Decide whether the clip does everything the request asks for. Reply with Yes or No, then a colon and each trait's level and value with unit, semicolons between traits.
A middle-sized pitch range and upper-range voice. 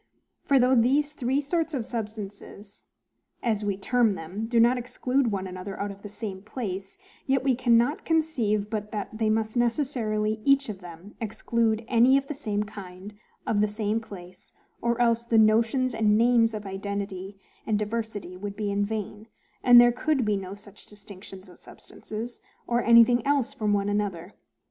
Yes: average, 3.0 semitones; high, 220 Hz